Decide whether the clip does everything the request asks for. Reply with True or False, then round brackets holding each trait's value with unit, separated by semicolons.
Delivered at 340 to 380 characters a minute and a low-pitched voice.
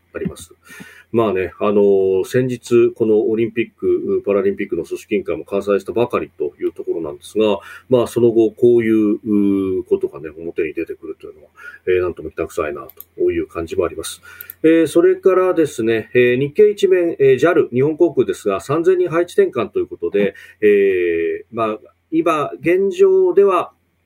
False (360 characters per minute; 360 Hz)